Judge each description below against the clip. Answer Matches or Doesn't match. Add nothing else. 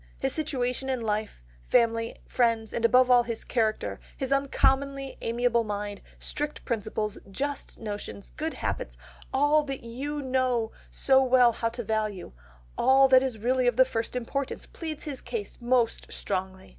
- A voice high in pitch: Matches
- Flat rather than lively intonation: Doesn't match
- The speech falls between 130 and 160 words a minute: Matches